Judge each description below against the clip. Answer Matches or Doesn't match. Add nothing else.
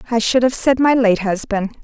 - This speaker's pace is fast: Matches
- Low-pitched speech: Doesn't match